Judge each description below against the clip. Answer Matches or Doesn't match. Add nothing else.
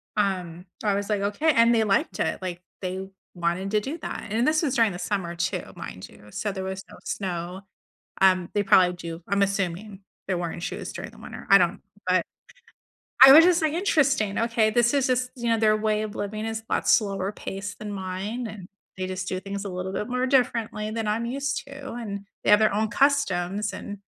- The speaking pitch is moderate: Doesn't match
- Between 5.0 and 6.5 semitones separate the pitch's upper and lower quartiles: Doesn't match